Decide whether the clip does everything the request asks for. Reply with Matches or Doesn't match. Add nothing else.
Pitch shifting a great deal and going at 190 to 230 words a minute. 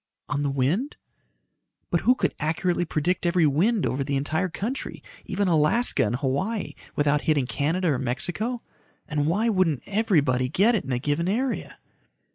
Doesn't match